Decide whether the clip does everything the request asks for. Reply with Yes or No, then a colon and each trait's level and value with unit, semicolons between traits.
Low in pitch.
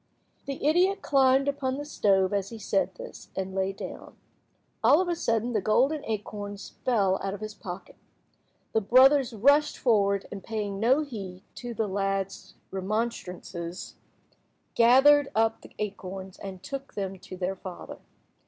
No: high, 210 Hz